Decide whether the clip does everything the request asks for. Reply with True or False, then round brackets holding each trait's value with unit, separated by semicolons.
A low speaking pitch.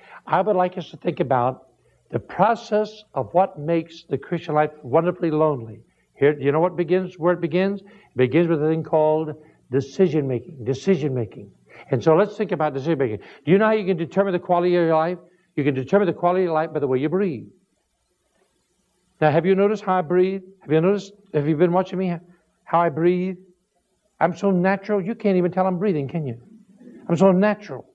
False (175 Hz)